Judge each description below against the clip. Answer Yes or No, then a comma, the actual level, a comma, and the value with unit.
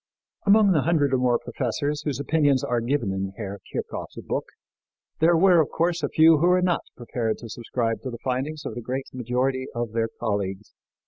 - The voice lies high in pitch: No, low, 130 Hz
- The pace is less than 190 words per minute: No, average, 195 wpm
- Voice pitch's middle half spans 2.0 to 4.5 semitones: No, average, 5.0 semitones